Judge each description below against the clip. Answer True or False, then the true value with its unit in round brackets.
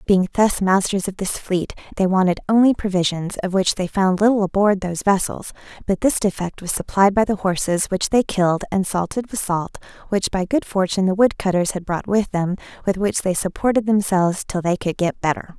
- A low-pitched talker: False (190 Hz)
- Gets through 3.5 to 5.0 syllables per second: False (5.5 syllables/s)